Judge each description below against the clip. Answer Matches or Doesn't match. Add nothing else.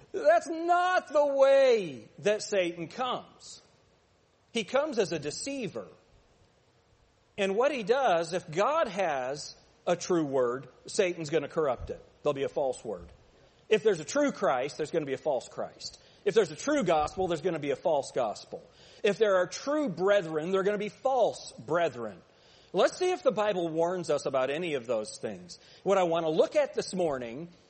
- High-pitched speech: Matches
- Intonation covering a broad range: Matches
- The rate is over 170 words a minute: Matches